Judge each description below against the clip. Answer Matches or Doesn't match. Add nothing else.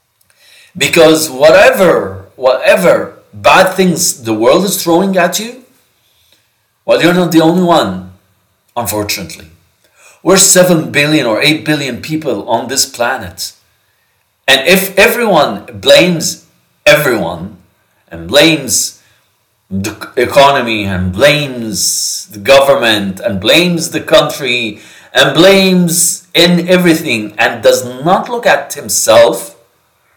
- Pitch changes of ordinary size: Doesn't match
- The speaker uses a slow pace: Matches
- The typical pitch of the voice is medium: Matches